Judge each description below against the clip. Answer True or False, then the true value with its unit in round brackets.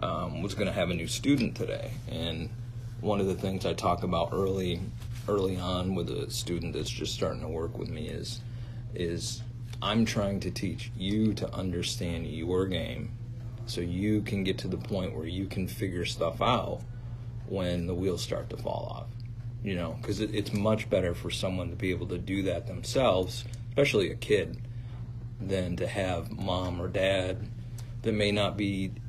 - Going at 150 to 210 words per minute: True (185 wpm)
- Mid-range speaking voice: False (105 Hz)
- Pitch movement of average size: True (3.8 semitones)